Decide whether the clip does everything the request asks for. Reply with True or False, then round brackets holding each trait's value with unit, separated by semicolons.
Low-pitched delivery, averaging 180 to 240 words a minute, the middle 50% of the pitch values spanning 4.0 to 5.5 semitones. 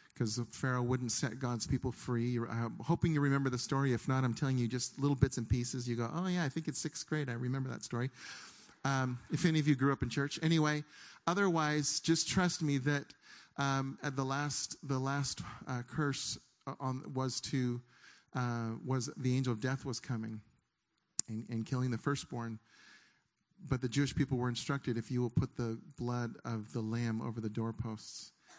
False (130 Hz; 195 wpm; 3.1 semitones)